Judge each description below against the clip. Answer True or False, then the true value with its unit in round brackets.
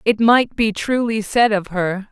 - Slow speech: False (200 wpm)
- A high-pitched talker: True (215 Hz)